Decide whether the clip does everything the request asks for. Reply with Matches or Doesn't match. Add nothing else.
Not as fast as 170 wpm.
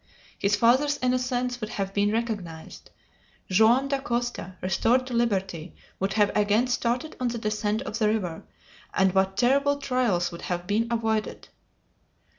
Matches